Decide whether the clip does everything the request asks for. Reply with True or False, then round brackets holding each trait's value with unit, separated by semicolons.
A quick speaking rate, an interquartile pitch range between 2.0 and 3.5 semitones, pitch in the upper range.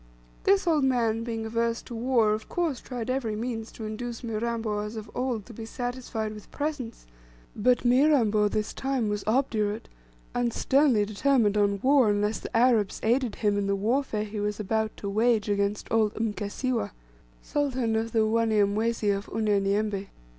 False (165 wpm; 2.7 semitones; 225 Hz)